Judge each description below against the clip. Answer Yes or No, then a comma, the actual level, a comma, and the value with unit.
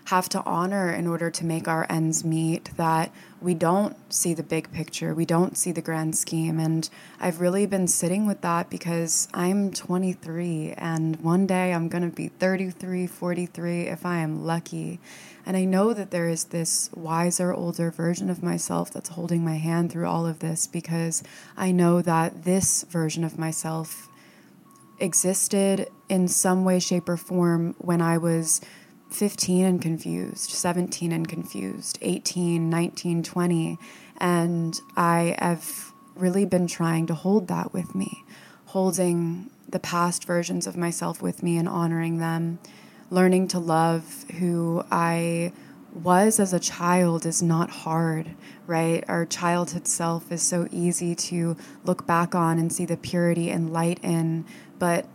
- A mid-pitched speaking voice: Yes, medium, 170 Hz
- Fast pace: No, average, 160 wpm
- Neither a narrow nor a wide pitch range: No, narrow, 1.6 semitones